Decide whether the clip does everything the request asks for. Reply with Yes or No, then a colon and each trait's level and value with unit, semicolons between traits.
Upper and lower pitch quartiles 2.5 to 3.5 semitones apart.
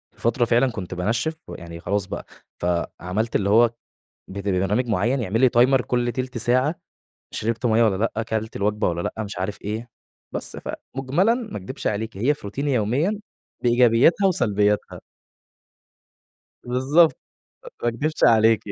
No: average, 3.9 semitones